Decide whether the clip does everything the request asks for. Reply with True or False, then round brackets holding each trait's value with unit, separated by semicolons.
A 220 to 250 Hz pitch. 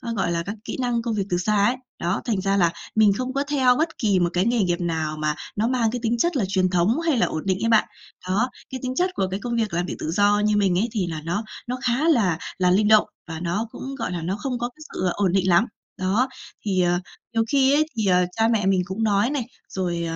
False (205 Hz)